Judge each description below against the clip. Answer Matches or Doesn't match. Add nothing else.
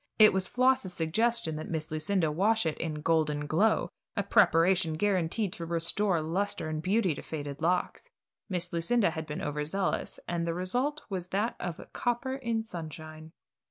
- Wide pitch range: Doesn't match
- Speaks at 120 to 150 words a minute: Doesn't match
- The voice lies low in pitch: Doesn't match